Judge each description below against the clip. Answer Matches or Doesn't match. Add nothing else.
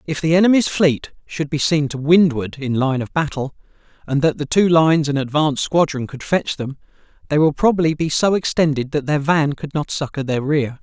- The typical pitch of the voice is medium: Matches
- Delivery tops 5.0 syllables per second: Matches